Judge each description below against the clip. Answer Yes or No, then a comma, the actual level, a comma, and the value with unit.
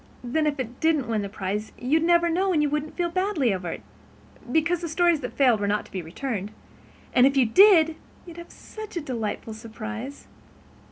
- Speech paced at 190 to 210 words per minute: Yes, fast, 205 wpm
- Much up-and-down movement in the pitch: Yes, wide, 7.1 semitones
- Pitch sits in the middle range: No, very high, 280 Hz